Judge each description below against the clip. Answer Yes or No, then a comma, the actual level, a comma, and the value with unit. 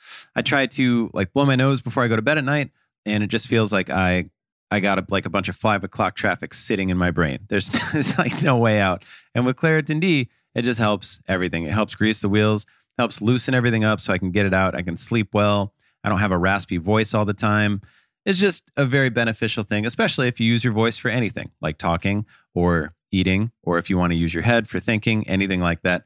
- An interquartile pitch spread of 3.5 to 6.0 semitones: Yes, average, 4.0 semitones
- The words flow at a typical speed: No, fast, 245 wpm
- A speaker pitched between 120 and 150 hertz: No, low, 105 Hz